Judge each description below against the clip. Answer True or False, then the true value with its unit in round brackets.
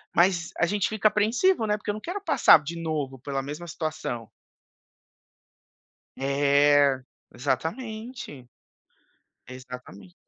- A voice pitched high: False (155 Hz)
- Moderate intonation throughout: False (7.5 semitones)